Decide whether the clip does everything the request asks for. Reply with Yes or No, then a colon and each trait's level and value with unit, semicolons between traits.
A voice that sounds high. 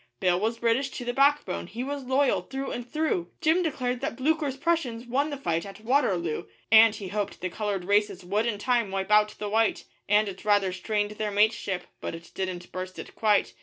Yes: high, 215 Hz